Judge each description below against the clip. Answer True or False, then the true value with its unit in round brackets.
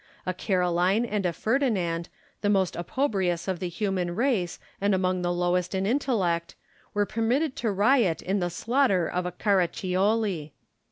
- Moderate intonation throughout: True (3.6 semitones)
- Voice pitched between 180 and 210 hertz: True (190 Hz)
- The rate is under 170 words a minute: True (155 wpm)